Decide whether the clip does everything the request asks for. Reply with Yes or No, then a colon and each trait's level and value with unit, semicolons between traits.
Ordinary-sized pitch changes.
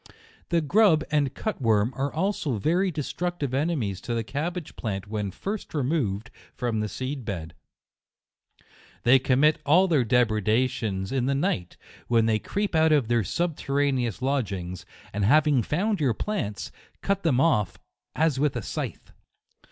No: wide, 6.3 semitones